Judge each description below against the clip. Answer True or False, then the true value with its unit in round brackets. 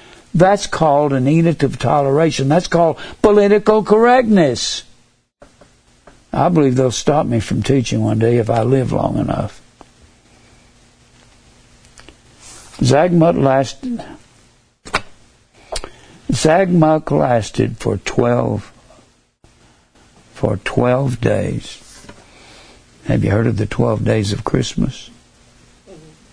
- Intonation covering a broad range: True (6.3 semitones)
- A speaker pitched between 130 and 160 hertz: True (135 Hz)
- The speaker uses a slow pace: True (95 wpm)